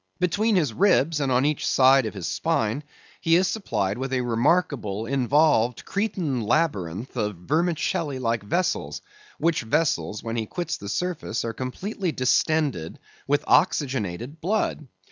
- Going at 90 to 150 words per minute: Yes, average, 145 wpm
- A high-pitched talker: No, low, 135 Hz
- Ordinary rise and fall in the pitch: No, wide, 6.5 semitones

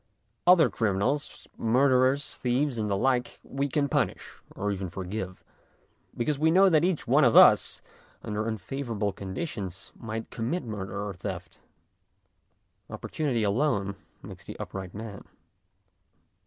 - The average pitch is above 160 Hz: No, low, 115 Hz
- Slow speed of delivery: Yes, slow, 130 wpm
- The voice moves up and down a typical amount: No, wide, 5.9 semitones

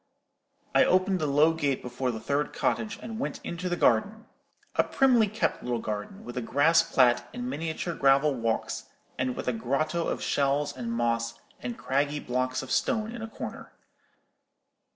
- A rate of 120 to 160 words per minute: No, average, 170 wpm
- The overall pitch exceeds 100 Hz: Yes, medium, 140 Hz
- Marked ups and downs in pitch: Yes, wide, 6.1 semitones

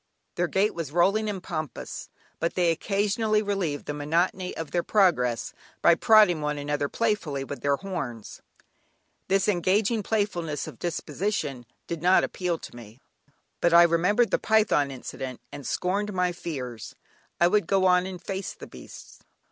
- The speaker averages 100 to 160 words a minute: Yes, average, 155 wpm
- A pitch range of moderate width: Yes, average, 5.0 semitones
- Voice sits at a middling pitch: Yes, medium, 175 Hz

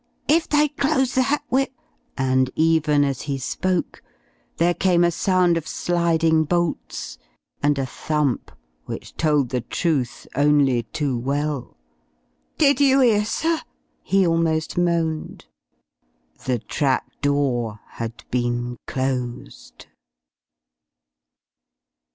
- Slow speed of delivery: Yes, slow, 110 wpm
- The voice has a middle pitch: Yes, medium, 155 Hz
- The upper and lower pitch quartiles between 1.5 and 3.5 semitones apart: No, average, 5.1 semitones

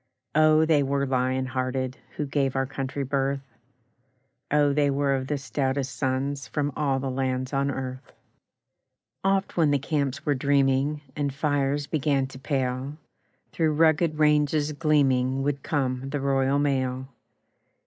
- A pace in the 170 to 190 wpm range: No, average, 145 wpm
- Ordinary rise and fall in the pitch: No, narrow, 1.8 semitones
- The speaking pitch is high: No, medium, 140 Hz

